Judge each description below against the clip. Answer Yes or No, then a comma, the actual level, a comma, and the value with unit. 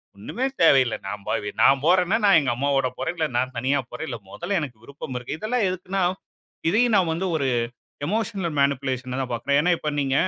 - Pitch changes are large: Yes, wide, 6.0 semitones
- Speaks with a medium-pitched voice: Yes, medium, 145 Hz